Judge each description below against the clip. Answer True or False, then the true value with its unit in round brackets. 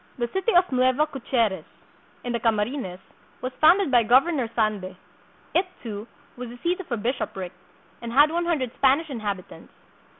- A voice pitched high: True (250 Hz)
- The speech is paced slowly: False (165 wpm)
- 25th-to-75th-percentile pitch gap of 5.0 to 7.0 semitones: True (5.6 semitones)